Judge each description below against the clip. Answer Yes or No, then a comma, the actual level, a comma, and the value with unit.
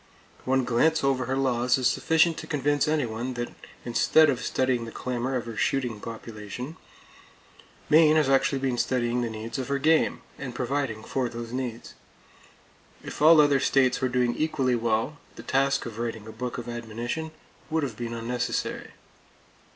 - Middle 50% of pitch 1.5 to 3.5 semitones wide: Yes, average, 2.8 semitones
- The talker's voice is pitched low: Yes, low, 125 Hz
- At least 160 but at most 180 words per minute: Yes, average, 165 wpm